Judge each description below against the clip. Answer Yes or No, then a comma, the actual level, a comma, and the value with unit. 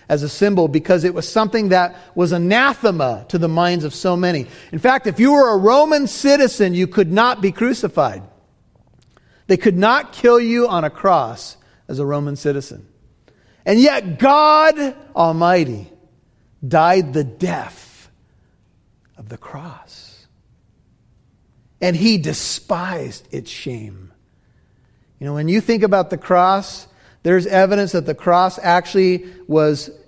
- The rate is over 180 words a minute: No, average, 140 wpm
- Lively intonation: Yes, wide, 5.9 semitones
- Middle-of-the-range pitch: Yes, medium, 180 Hz